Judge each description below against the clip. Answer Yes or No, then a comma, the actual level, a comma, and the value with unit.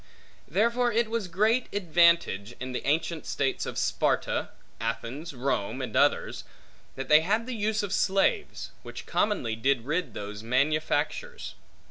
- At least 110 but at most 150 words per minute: Yes, average, 140 wpm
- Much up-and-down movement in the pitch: Yes, wide, 8.4 semitones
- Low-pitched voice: No, medium, 160 Hz